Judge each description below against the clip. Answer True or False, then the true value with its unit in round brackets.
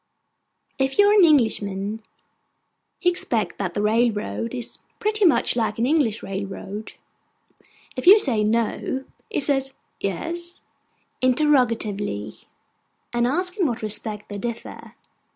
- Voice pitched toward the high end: True (235 Hz)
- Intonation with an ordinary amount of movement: False (6.3 semitones)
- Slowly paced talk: True (125 wpm)